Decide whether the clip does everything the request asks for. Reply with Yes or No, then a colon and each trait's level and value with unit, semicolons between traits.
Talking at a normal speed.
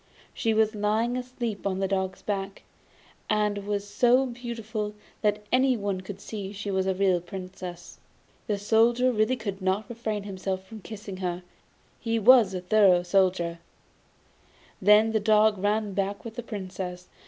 Yes: average, 155 wpm